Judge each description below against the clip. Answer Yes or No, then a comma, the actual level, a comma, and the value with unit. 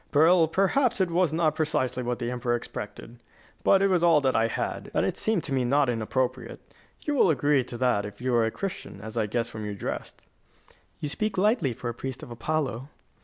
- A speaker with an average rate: No, fast, 220 wpm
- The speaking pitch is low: Yes, low, 130 Hz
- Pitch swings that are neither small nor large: No, wide, 6.0 semitones